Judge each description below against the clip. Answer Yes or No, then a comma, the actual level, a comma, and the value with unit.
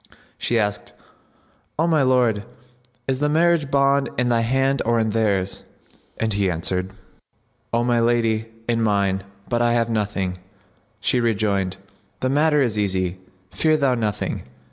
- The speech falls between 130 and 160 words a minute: Yes, average, 145 wpm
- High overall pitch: No, low, 115 Hz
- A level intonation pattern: No, average, 4.4 semitones